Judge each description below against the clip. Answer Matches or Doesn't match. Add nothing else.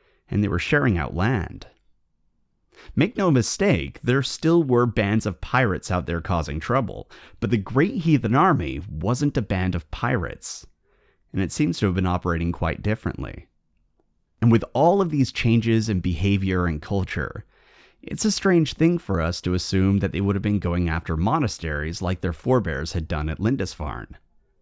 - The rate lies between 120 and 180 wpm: Matches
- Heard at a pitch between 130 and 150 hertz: Doesn't match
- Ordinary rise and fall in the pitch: Doesn't match